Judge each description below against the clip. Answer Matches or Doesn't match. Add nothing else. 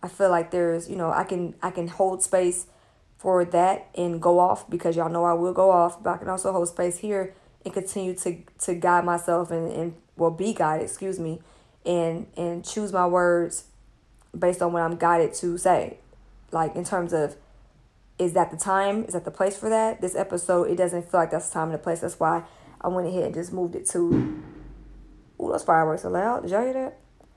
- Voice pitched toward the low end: Doesn't match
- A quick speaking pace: Matches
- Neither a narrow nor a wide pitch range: Doesn't match